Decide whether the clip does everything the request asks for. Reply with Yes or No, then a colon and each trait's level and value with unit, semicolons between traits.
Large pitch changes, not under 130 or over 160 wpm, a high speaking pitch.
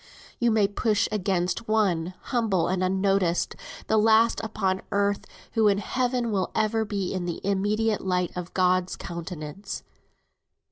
No: average, 3.0 semitones; average, 145 wpm; high, 200 Hz